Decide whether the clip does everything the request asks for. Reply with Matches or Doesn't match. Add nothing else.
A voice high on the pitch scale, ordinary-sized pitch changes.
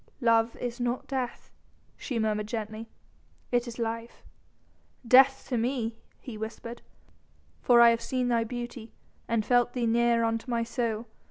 Doesn't match